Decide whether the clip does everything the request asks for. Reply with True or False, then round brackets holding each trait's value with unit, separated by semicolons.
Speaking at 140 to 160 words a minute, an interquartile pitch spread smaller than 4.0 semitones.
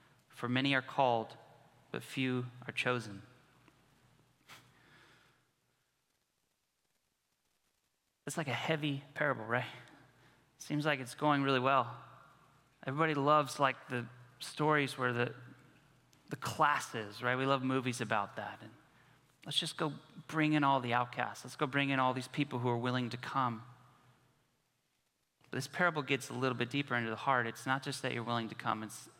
True (155 wpm; 2.6 semitones)